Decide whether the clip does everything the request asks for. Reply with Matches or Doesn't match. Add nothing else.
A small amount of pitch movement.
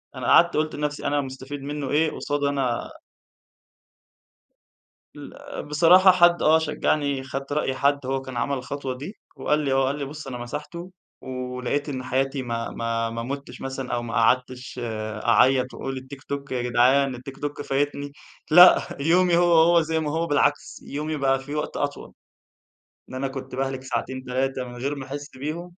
Matches